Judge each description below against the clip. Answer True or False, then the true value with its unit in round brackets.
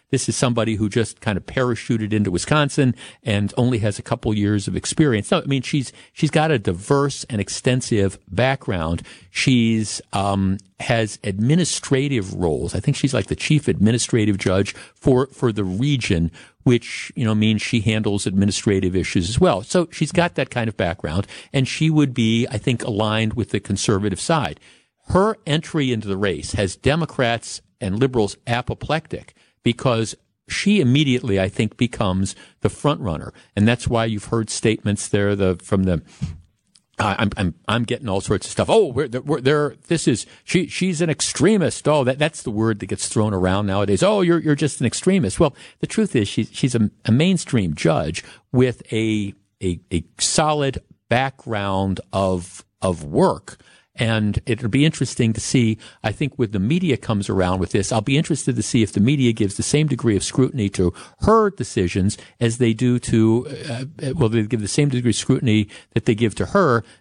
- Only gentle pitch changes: False (4.8 semitones)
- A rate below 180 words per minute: False (185 wpm)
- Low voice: True (115 Hz)